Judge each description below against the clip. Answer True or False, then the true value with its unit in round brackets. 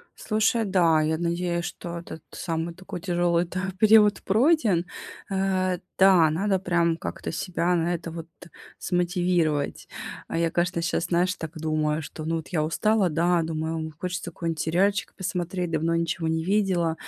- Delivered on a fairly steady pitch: True (2.2 semitones)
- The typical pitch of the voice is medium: True (175 Hz)